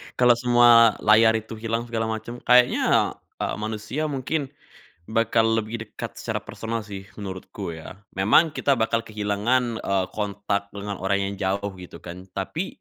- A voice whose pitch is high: No, low, 110 Hz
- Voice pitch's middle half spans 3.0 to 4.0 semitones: No, narrow, 2.6 semitones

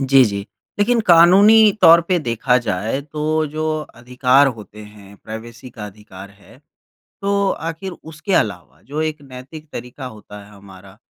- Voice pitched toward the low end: Yes, low, 130 Hz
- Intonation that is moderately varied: No, wide, 6.9 semitones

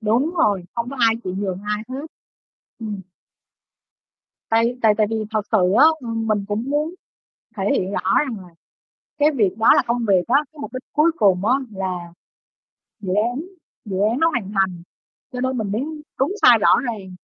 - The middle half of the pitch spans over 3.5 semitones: Yes, average, 4.6 semitones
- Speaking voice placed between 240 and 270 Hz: No, high, 220 Hz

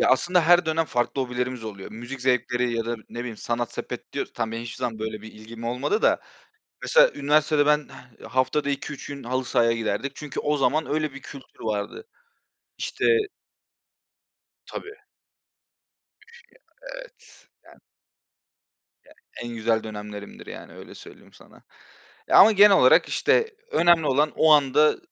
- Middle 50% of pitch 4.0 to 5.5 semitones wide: Yes, average, 4.7 semitones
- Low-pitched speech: Yes, low, 130 Hz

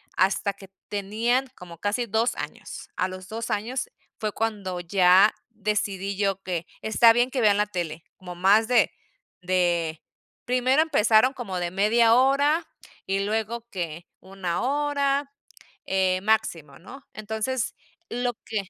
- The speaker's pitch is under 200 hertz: No, high, 210 Hz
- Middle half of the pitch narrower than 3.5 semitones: No, average, 4.2 semitones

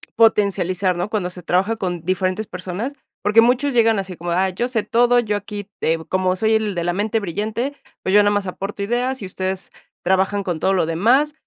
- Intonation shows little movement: No, average, 3.3 semitones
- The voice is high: Yes, high, 200 Hz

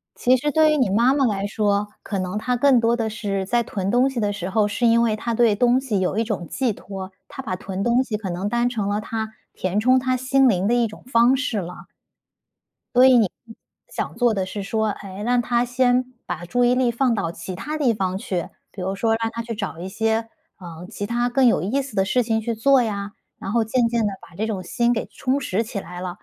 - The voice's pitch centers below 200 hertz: No, high, 225 Hz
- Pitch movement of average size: Yes, average, 3.6 semitones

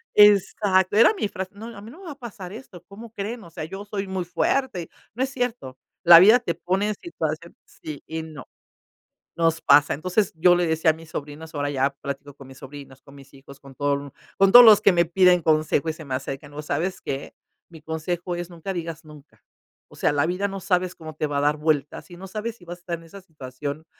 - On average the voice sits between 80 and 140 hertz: No, medium, 170 Hz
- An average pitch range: Yes, average, 4.9 semitones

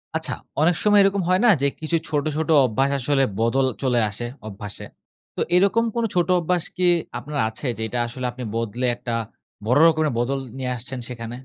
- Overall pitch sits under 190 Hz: Yes, low, 135 Hz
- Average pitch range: No, wide, 5.7 semitones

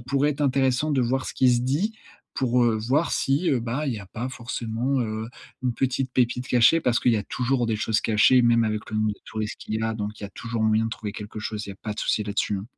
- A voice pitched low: Yes, low, 120 Hz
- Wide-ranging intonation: No, average, 3.1 semitones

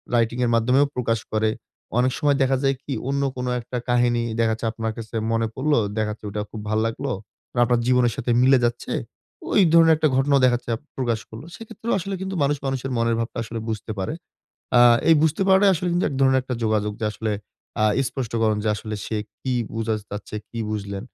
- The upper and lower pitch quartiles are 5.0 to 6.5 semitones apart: No, average, 3.3 semitones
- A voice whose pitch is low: Yes, low, 120 Hz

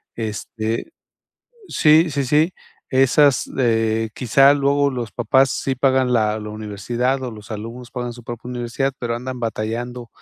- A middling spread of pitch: Yes, average, 3.0 semitones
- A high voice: No, low, 120 Hz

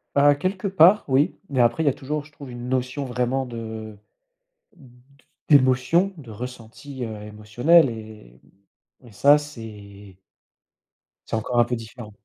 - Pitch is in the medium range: No, low, 125 Hz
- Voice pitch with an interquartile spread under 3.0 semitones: No, average, 4.4 semitones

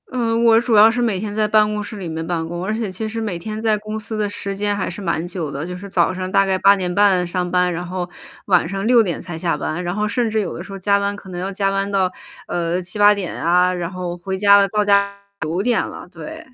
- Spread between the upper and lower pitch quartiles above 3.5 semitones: No, average, 2.9 semitones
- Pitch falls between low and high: No, high, 195 Hz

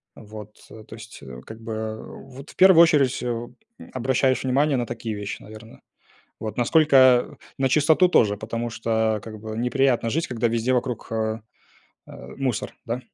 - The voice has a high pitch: No, low, 115 Hz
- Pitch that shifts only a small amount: No, average, 3.0 semitones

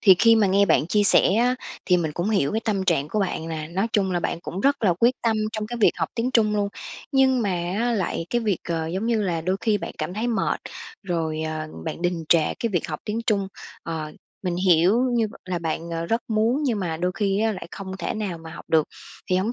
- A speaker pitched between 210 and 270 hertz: No, high, 195 Hz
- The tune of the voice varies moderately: Yes, average, 4.6 semitones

